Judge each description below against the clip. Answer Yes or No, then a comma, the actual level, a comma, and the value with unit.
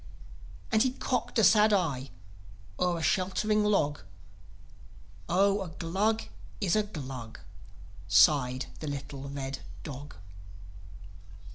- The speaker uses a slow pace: Yes, slow, 110 wpm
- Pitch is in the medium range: Yes, medium, 165 Hz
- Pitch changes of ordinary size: No, wide, 7.0 semitones